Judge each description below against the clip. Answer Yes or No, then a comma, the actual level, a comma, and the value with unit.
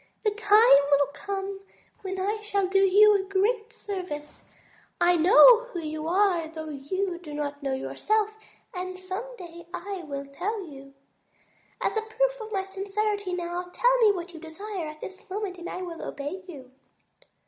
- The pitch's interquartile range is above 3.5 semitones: Yes, average, 4.2 semitones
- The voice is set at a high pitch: Yes, very high, 375 Hz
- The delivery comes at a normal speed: Yes, average, 170 wpm